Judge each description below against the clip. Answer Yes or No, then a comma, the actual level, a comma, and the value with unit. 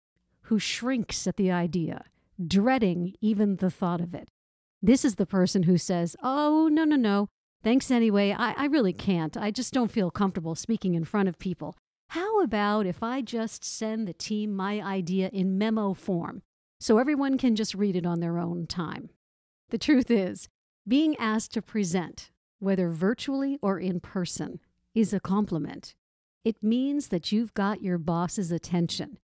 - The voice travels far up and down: No, average, 4.1 semitones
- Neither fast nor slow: Yes, average, 170 wpm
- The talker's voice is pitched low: No, high, 200 Hz